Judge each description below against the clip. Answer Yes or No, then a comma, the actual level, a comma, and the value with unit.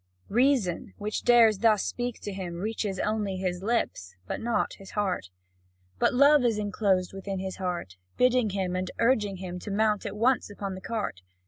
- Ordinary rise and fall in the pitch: Yes, average, 3.3 semitones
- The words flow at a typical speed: Yes, average, 180 wpm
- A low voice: No, high, 205 Hz